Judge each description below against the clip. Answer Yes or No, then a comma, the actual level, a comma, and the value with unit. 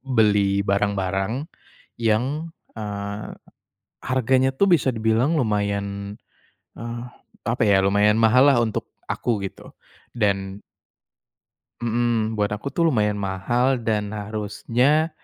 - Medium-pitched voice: No, low, 110 Hz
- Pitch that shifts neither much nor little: Yes, average, 3.2 semitones